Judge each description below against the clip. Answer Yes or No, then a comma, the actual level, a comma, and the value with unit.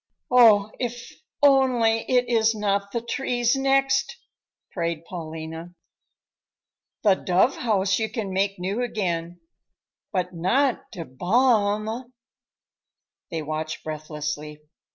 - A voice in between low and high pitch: No, high, 205 Hz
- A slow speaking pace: Yes, slow, 105 wpm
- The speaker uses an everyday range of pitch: No, wide, 6.1 semitones